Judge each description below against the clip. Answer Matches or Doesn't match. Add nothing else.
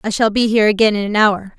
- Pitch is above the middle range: Matches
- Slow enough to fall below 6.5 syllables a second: Doesn't match